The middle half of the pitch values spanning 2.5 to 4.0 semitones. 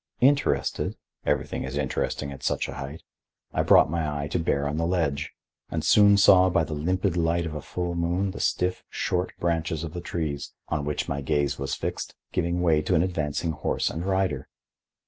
Yes: average, 3.4 semitones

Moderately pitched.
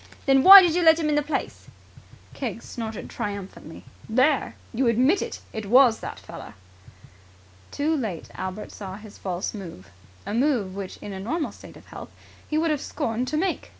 No: high, 235 Hz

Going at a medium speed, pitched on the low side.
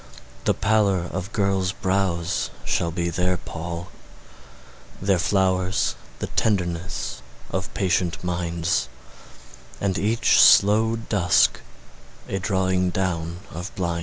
No: slow, 105 wpm; very low, 90 Hz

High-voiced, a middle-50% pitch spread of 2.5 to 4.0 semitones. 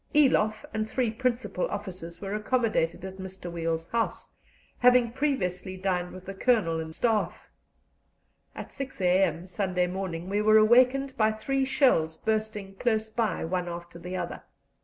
No: high, 200 Hz; average, 4.5 semitones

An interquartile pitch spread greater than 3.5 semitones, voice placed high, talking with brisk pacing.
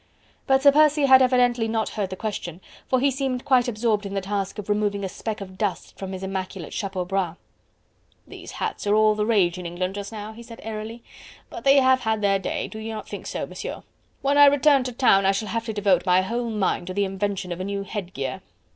Yes: average, 3.9 semitones; high, 210 Hz; fast, 235 wpm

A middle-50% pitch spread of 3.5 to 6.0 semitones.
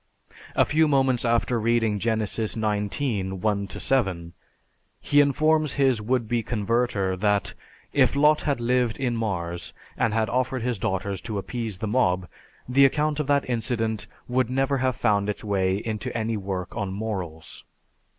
Yes: average, 4.2 semitones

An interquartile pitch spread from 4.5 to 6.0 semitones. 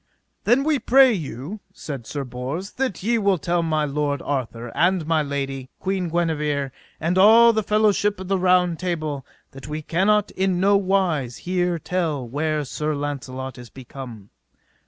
Yes: average, 5.3 semitones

